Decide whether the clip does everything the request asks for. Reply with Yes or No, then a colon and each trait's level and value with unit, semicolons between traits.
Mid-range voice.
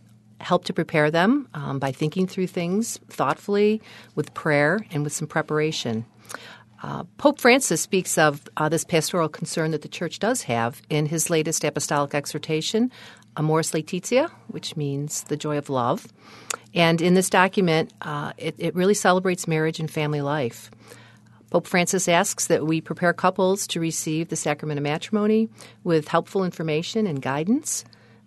Yes: medium, 160 Hz